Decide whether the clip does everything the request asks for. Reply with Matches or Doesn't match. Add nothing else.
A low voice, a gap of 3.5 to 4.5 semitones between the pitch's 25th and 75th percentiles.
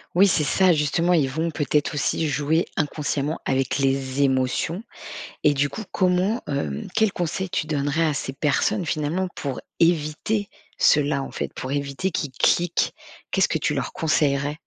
Doesn't match